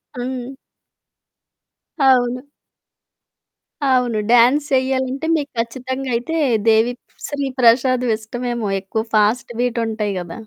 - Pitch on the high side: Yes, high, 245 Hz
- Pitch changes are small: Yes, narrow, 2.1 semitones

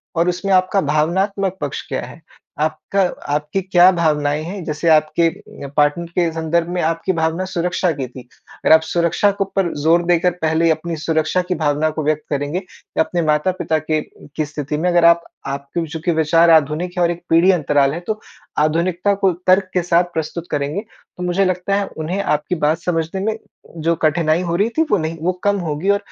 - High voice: No, medium, 170 Hz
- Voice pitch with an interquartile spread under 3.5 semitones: Yes, average, 2.8 semitones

